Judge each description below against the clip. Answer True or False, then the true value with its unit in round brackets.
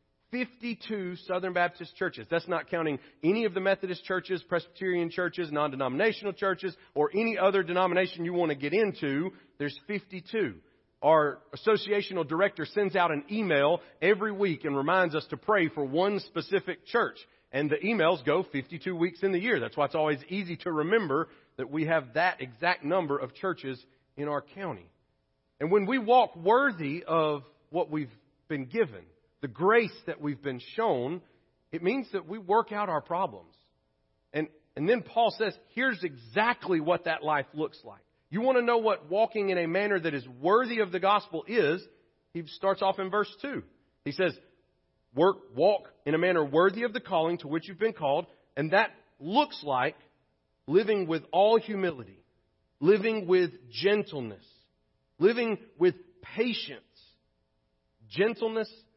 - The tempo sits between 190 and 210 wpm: False (165 wpm)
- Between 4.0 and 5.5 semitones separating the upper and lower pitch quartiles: True (5.1 semitones)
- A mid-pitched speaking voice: True (180 Hz)